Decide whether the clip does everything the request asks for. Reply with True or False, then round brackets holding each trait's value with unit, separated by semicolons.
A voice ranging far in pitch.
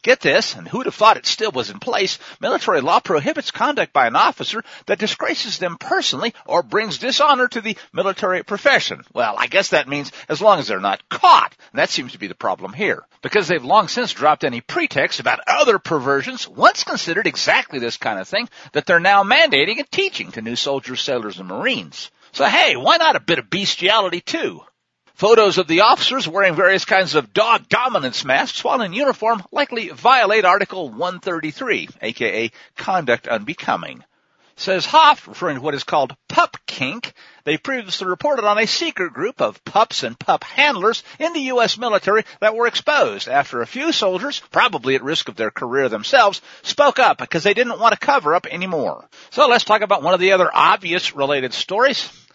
True (6.9 semitones)